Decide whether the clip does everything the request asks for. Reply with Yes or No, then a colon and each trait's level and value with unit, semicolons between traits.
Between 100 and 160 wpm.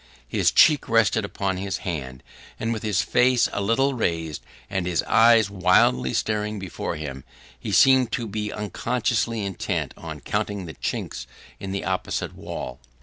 Yes: average, 155 wpm